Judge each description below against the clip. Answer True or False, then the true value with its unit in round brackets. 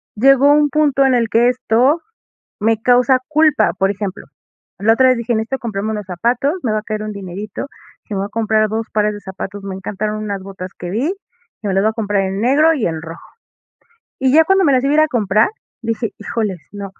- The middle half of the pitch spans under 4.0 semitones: False (4.3 semitones)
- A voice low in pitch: False (220 Hz)